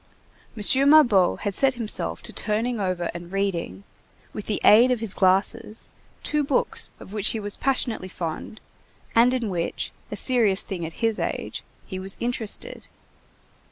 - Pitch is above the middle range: Yes, high, 210 Hz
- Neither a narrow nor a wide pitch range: Yes, average, 4.2 semitones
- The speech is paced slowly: No, average, 155 wpm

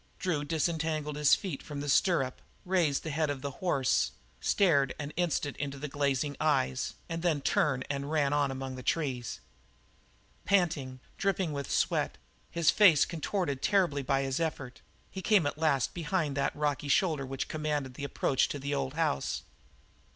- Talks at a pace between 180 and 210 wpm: No, average, 165 wpm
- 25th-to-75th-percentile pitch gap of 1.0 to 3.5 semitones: Yes, average, 3.0 semitones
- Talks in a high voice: No, medium, 145 Hz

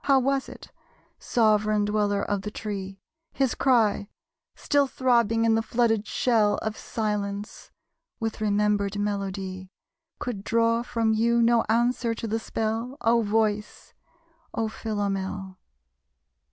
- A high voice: Yes, high, 220 Hz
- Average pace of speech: No, slow, 125 wpm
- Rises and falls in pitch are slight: Yes, narrow, 2.1 semitones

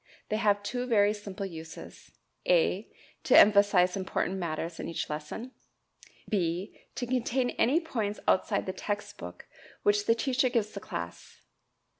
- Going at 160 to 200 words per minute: No, average, 145 wpm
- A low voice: No, high, 205 Hz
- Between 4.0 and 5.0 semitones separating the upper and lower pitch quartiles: Yes, average, 4.6 semitones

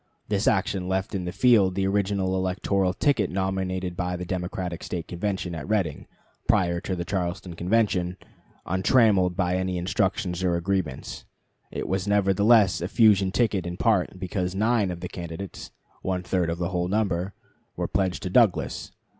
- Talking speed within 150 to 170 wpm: Yes, average, 165 wpm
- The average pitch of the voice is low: Yes, very low, 95 Hz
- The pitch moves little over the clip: Yes, narrow, 1.7 semitones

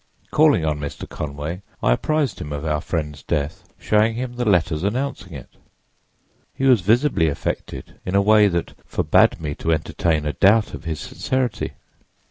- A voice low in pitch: Yes, very low, 85 Hz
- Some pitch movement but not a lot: No, wide, 7.0 semitones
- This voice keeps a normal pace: Yes, average, 165 wpm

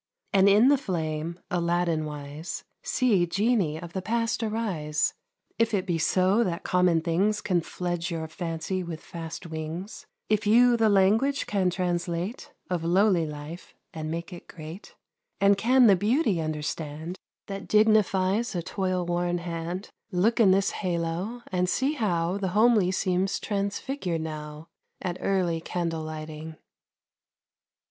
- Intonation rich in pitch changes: No, average, 3.7 semitones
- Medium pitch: Yes, medium, 180 Hz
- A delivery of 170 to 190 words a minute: No, average, 140 wpm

